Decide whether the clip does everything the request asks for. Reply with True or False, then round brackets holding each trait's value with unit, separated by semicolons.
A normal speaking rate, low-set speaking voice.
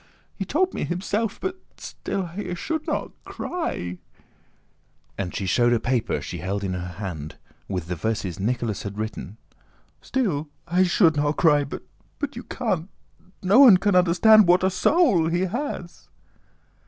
False (150 wpm; 170 Hz)